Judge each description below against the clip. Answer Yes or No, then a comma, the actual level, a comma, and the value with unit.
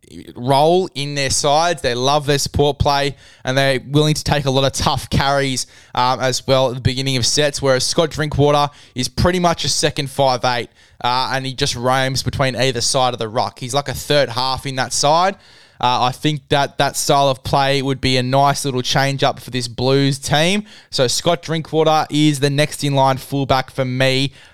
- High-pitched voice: No, low, 135 Hz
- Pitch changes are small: Yes, narrow, 2.1 semitones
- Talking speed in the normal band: No, fast, 210 wpm